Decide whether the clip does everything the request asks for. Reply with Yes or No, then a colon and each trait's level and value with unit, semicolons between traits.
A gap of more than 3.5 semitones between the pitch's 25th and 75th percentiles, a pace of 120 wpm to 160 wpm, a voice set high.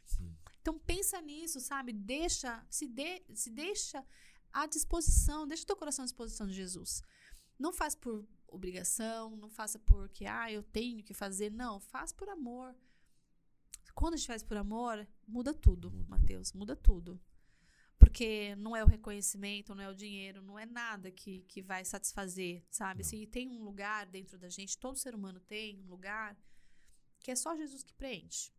No: average, 5.1 semitones; average, 170 wpm; high, 220 Hz